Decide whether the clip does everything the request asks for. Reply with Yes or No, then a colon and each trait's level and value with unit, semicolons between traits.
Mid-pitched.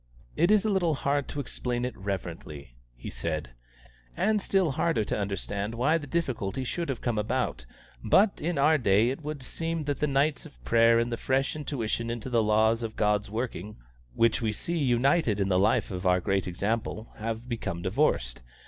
No: low, 115 Hz